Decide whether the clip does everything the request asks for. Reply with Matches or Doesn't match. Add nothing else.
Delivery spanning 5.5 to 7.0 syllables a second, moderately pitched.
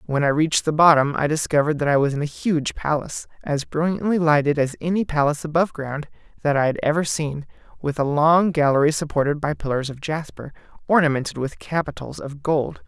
Matches